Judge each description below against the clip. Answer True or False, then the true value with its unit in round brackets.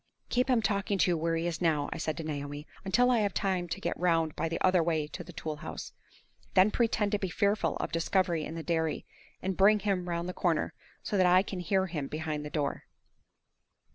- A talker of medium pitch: True (175 Hz)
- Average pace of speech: False (230 wpm)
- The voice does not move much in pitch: False (3.4 semitones)